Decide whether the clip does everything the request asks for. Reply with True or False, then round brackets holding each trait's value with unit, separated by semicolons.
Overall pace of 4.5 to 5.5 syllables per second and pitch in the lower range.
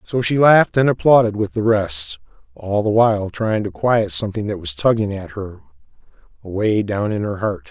True (5.2 syllables/s; 110 Hz)